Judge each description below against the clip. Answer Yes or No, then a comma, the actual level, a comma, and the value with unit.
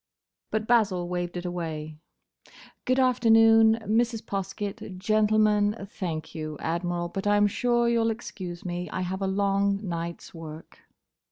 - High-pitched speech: Yes, high, 195 Hz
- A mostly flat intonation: No, average, 3.8 semitones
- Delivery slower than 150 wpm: Yes, average, 140 wpm